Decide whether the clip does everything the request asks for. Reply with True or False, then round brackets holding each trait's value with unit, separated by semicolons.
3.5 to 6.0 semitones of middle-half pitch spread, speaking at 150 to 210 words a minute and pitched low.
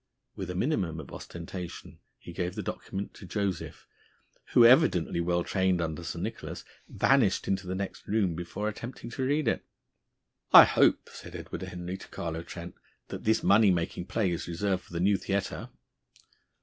False (3.0 semitones; 170 wpm; 95 Hz)